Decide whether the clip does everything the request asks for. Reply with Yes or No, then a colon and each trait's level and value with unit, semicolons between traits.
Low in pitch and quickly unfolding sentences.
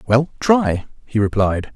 No: low, 120 Hz; slow, 135 wpm